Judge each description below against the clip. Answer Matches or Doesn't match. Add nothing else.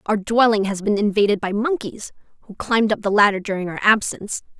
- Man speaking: Doesn't match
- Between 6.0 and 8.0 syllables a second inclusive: Matches